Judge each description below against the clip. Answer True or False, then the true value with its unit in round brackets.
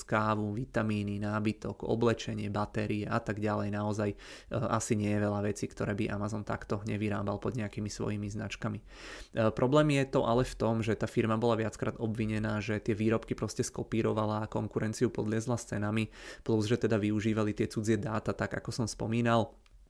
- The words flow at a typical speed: False (175 wpm)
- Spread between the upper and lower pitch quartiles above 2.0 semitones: False (1.7 semitones)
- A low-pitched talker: True (110 Hz)